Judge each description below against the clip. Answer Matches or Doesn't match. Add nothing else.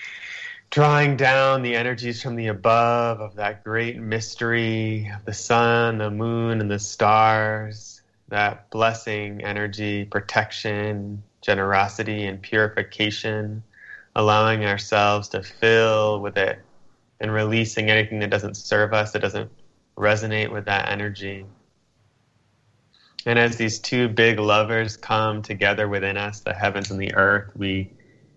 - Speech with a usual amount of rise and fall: Doesn't match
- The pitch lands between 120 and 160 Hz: Doesn't match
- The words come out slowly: Matches